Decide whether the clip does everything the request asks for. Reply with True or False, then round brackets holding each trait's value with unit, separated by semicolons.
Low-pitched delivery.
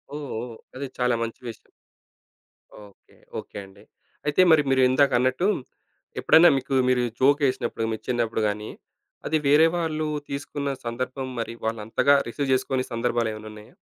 True (130 Hz)